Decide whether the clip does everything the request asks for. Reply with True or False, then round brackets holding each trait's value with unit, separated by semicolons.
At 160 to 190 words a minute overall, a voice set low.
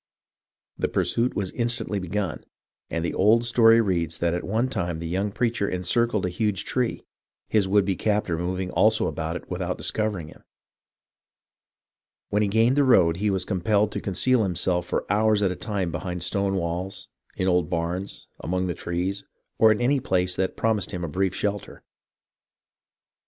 True (175 wpm; 95 Hz)